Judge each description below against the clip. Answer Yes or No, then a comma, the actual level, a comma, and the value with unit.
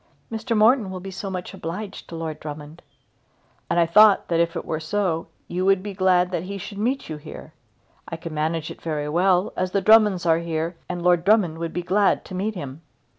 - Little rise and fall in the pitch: No, average, 3.3 semitones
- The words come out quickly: Yes, fast, 220 wpm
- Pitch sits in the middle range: Yes, medium, 180 Hz